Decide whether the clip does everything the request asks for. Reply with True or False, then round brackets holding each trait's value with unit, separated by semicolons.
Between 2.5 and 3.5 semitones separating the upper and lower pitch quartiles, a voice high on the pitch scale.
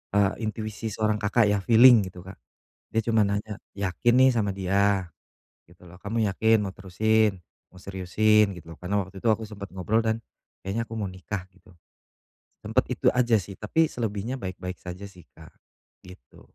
False (2.8 semitones; 100 Hz)